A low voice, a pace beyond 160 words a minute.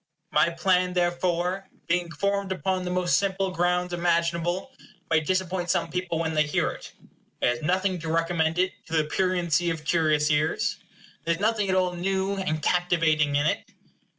No: medium, 175 Hz; average, 175 wpm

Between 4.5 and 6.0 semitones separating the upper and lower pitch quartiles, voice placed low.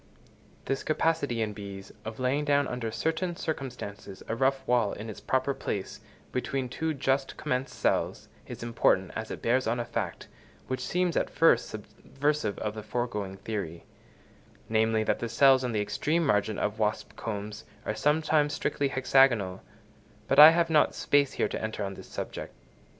Yes: average, 4.8 semitones; low, 125 Hz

